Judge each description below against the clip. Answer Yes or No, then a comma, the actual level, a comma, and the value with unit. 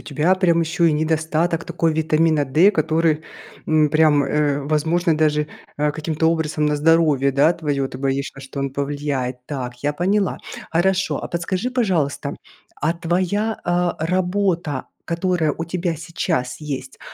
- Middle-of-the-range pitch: Yes, medium, 160 Hz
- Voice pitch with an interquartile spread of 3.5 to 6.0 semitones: No, average, 2.8 semitones